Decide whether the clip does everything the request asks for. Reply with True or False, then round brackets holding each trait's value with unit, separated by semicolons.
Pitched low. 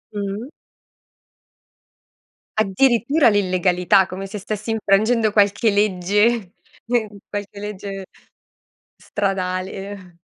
False (205 Hz)